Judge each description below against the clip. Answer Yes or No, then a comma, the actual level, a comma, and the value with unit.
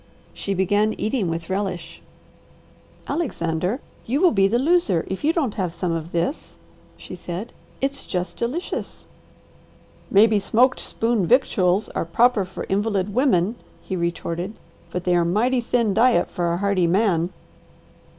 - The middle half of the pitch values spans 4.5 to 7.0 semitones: Yes, average, 5.1 semitones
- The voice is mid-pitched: No, high, 200 Hz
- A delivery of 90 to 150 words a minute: Yes, average, 145 wpm